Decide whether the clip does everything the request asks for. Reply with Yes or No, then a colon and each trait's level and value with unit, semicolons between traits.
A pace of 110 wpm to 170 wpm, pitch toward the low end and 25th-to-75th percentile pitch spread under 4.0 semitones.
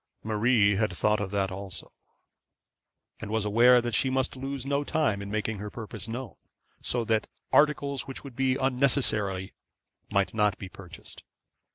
No: average, 160 wpm; low, 110 Hz; average, 4.5 semitones